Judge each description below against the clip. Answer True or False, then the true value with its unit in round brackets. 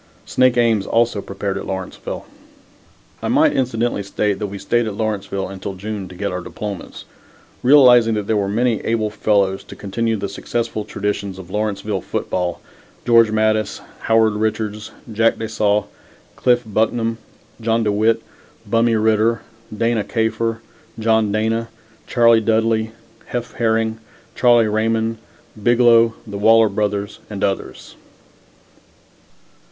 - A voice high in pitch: False (110 Hz)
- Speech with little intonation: True (2.0 semitones)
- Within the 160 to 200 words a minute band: False (135 wpm)